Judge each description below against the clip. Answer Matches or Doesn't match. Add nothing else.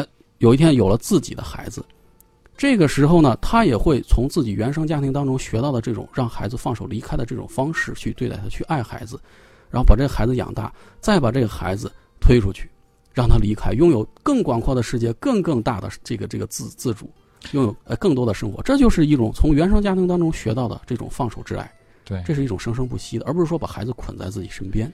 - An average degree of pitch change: Matches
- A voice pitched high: Doesn't match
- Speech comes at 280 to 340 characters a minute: Doesn't match